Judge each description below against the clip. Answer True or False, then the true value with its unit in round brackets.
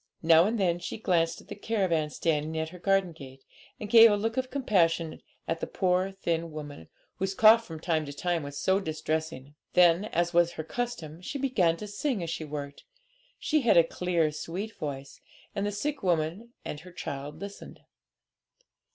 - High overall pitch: False (175 Hz)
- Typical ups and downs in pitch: True (4.3 semitones)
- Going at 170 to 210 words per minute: True (185 wpm)